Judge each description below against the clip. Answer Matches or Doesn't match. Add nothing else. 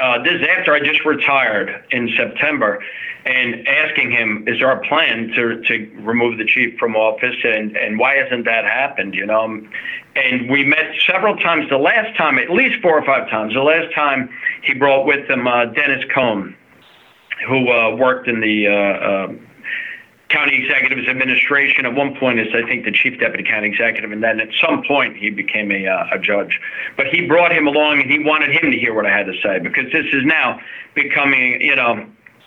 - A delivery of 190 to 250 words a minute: Matches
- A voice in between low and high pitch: Doesn't match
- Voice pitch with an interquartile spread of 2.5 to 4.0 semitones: Doesn't match